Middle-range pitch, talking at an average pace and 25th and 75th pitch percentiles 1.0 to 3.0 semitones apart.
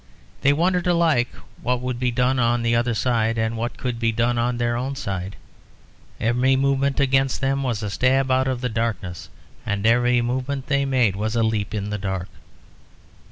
No: low, 120 Hz; average, 190 wpm; average, 2.7 semitones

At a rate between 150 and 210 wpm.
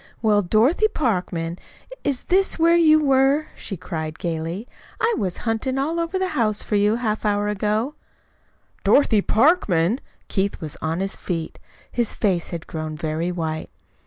Yes: average, 160 wpm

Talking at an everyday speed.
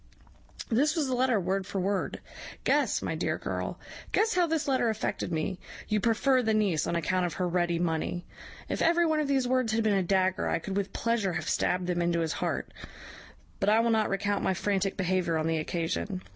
No: fast, 215 wpm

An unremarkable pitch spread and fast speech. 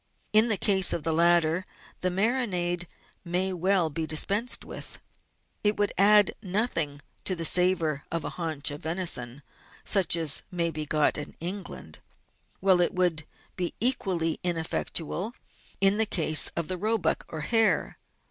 No: average, 3.4 semitones; average, 150 wpm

